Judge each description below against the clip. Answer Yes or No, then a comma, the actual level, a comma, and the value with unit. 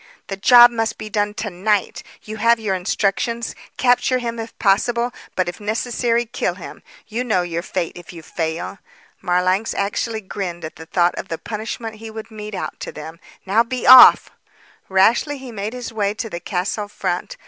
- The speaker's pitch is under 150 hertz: No, high, 210 Hz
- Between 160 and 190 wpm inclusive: Yes, average, 185 wpm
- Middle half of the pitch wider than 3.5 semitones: Yes, average, 4.0 semitones